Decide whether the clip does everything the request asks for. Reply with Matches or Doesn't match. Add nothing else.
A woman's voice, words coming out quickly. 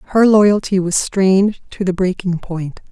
Doesn't match